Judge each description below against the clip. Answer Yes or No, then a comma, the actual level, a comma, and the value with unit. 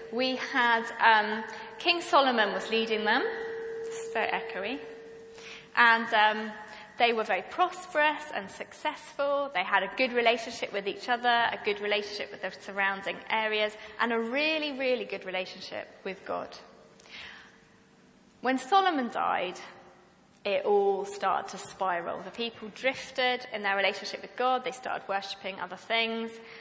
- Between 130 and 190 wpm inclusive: Yes, average, 140 wpm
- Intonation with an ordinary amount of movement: Yes, average, 4.4 semitones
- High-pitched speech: Yes, high, 225 Hz